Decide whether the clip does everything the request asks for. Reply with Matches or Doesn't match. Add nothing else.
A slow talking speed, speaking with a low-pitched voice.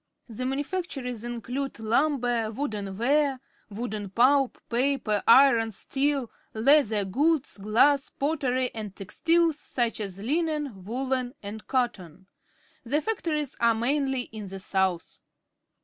Doesn't match